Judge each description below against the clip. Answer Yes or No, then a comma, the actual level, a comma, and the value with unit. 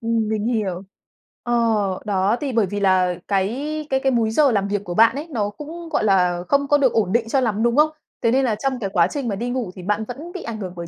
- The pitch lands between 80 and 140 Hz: No, high, 225 Hz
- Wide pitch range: No, average, 4.8 semitones